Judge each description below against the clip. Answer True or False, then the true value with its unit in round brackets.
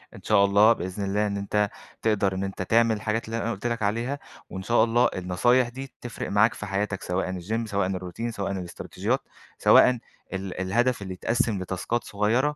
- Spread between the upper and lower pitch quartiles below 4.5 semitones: True (3.3 semitones)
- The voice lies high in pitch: False (105 Hz)